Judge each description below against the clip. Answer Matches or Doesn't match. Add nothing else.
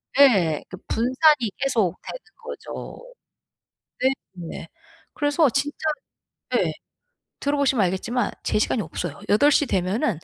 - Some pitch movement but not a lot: Doesn't match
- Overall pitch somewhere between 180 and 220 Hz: Doesn't match